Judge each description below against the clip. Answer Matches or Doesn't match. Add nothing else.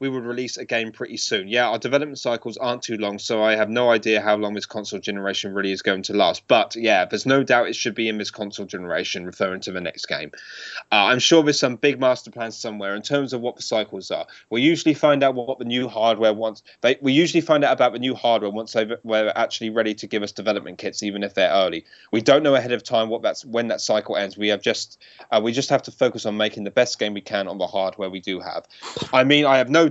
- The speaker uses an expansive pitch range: Doesn't match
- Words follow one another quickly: Matches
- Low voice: Matches